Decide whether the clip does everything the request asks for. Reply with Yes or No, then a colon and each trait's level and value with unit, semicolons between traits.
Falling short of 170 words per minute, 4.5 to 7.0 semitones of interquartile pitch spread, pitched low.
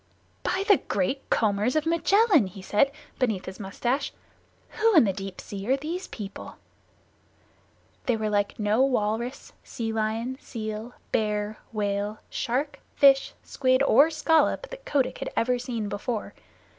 No: average, 145 wpm; average, 4.9 semitones; high, 235 Hz